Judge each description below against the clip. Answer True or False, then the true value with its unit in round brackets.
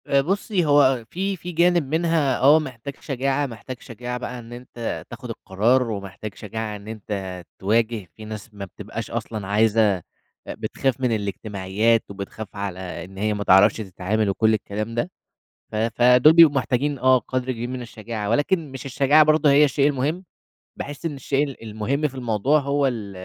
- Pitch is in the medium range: False (120 Hz)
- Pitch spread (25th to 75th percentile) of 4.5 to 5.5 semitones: True (4.8 semitones)